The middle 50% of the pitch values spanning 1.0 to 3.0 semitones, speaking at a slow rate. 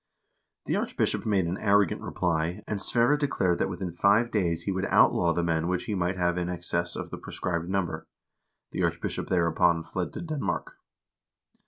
No: narrow, 2.6 semitones; average, 175 wpm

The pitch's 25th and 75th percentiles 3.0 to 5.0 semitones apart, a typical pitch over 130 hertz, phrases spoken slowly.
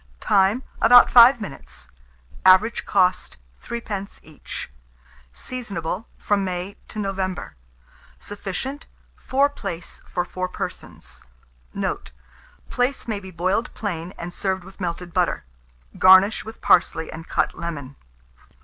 Yes: average, 3.8 semitones; high, 190 Hz; slow, 115 wpm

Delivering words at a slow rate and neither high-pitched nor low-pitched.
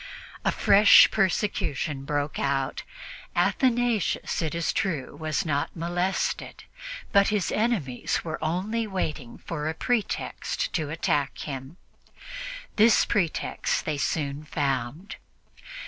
Yes: slow, 110 wpm; medium, 160 Hz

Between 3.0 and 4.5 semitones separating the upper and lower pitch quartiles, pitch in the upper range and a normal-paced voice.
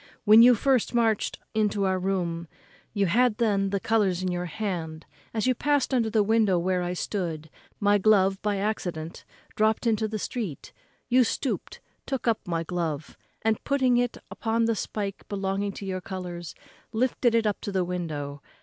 Yes: average, 3.8 semitones; high, 205 Hz; average, 175 wpm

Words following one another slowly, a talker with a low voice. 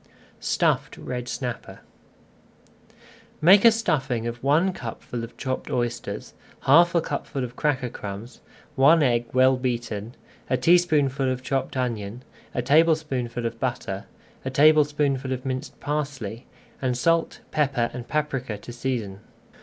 Yes: slow, 130 wpm; low, 130 Hz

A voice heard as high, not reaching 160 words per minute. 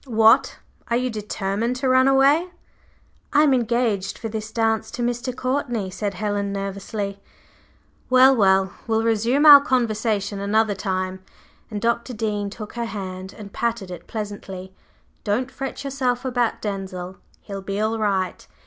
Yes: high, 220 Hz; average, 150 wpm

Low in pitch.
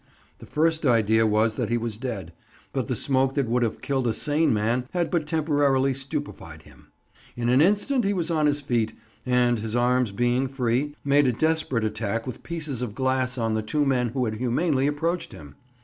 Yes: low, 130 Hz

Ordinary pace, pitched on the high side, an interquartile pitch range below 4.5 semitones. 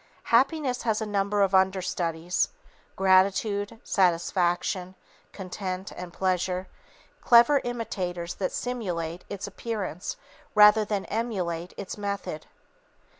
No: slow, 105 wpm; high, 195 Hz; average, 2.8 semitones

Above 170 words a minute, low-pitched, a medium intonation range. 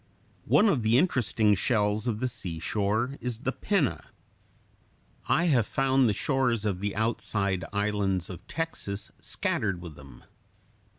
No: slow, 135 wpm; low, 110 Hz; average, 4.4 semitones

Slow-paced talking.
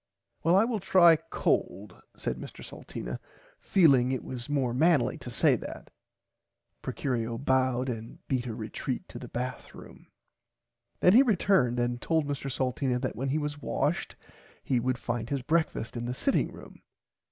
No: average, 165 wpm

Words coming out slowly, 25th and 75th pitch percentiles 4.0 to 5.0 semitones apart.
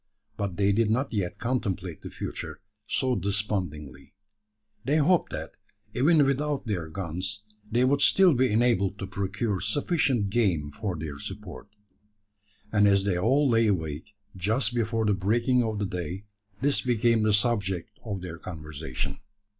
No: average, 150 wpm; average, 4.5 semitones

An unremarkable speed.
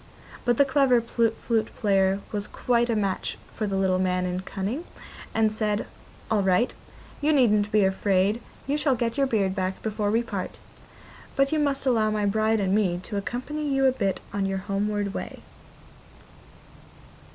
Yes: average, 170 wpm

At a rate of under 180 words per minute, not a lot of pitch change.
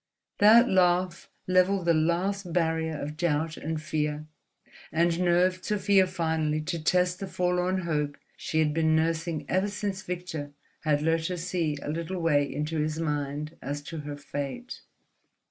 No: average, 155 wpm; average, 3.0 semitones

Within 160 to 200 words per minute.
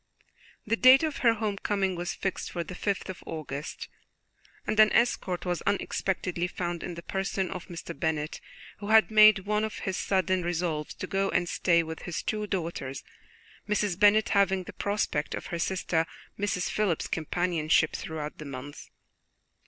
Yes: average, 165 wpm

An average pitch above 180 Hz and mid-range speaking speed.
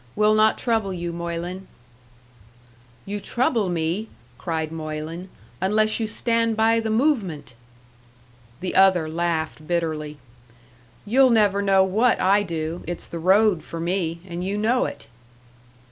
No: high, 190 Hz; slow, 130 wpm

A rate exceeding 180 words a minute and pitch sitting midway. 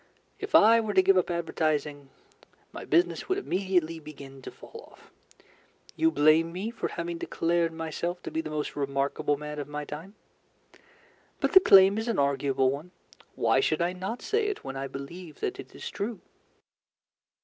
No: average, 175 wpm; medium, 165 Hz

